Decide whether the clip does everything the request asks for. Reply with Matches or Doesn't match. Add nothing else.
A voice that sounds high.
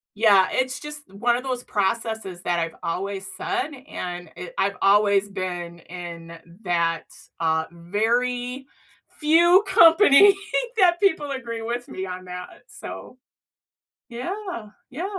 Matches